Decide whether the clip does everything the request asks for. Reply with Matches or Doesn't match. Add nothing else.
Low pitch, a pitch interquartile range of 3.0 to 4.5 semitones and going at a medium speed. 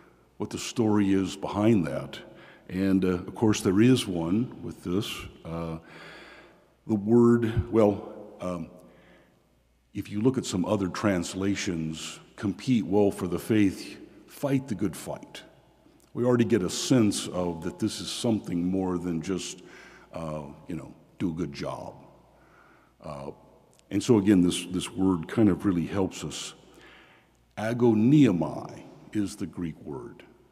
Matches